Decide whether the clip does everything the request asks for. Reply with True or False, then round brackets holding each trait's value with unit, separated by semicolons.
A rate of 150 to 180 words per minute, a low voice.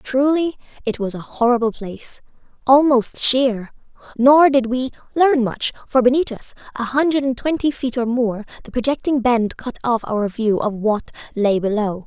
False (170 wpm; 245 Hz)